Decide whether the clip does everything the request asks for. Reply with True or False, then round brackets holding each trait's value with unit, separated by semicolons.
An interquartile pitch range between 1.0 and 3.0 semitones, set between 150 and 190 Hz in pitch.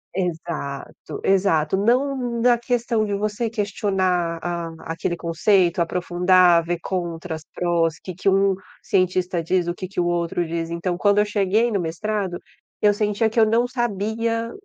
False (3.7 semitones; 185 Hz)